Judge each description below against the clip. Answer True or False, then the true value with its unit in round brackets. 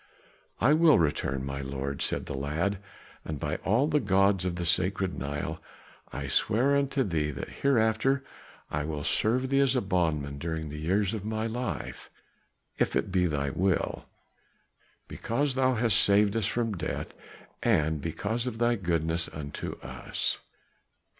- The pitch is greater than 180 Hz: False (95 Hz)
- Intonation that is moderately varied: False (7.1 semitones)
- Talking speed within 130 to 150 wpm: False (160 wpm)